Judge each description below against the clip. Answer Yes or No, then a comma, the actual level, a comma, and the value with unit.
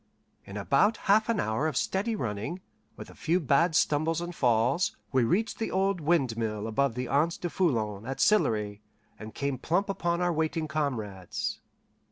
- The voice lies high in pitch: No, medium, 150 Hz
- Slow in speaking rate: No, average, 170 wpm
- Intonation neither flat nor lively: No, wide, 7.6 semitones